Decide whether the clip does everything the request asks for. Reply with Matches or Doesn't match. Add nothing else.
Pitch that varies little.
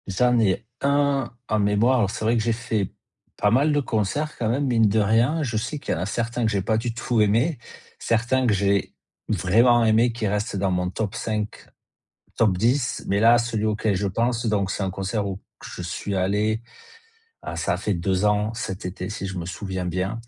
Doesn't match